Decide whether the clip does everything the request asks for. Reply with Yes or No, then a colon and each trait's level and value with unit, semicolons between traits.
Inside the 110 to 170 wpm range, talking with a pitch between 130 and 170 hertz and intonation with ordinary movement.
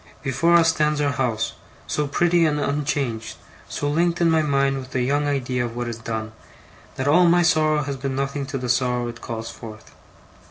No: average, 200 wpm; medium, 140 Hz; average, 3.6 semitones